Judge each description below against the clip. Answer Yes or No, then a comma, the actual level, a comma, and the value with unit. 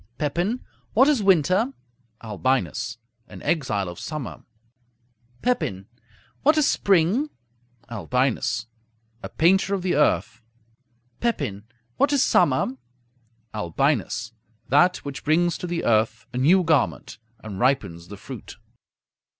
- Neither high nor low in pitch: Yes, medium, 145 Hz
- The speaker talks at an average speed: No, slow, 115 wpm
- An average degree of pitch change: No, wide, 8.6 semitones